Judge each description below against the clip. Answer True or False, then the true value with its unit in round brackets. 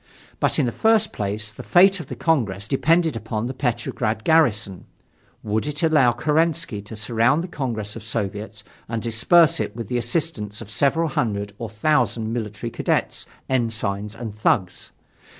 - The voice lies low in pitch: True (115 Hz)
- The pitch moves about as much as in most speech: False (5.9 semitones)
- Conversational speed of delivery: True (160 wpm)